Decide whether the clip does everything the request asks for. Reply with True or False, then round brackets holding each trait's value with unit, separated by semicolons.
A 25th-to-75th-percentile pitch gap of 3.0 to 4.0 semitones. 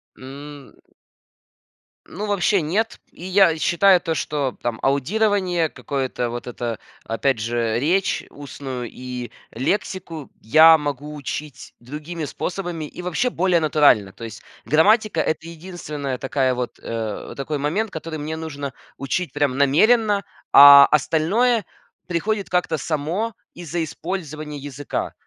False (4.6 semitones)